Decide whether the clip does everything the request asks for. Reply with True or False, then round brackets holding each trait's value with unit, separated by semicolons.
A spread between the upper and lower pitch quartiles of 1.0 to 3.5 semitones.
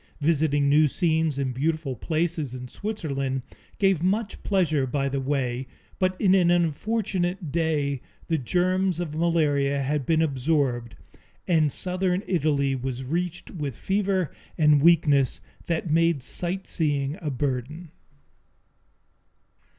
False (4.1 semitones)